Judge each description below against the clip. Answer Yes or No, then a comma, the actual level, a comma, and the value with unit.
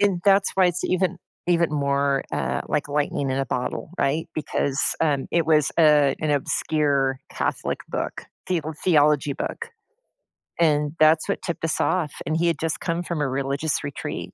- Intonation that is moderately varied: Yes, average, 3.2 semitones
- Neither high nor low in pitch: Yes, medium, 150 Hz